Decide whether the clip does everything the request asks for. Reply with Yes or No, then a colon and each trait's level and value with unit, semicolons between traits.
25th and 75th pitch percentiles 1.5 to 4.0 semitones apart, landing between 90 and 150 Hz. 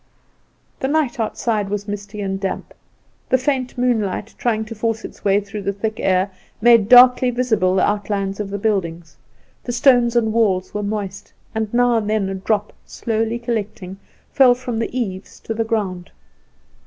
No: average, 3.2 semitones; high, 215 Hz